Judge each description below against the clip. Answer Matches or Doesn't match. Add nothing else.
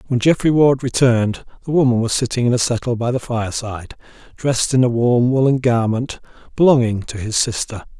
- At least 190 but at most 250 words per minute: Doesn't match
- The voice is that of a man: Matches